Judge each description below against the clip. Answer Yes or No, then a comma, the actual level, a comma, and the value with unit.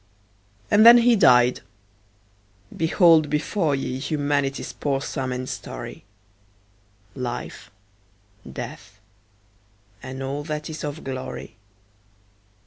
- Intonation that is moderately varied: Yes, average, 3.3 semitones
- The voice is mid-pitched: Yes, medium, 145 Hz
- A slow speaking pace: Yes, slow, 95 wpm